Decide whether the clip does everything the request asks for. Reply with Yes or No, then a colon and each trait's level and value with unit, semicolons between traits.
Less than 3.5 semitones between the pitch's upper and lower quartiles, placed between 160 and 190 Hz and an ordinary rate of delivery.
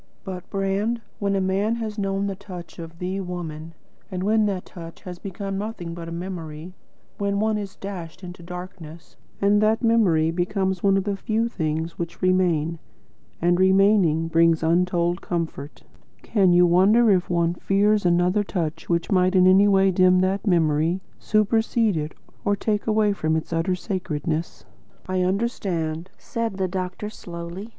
Yes: average, 2.9 semitones; medium, 185 Hz; average, 160 wpm